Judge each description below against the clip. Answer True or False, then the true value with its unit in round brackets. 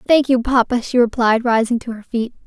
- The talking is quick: True (220 wpm)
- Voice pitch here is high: True (240 Hz)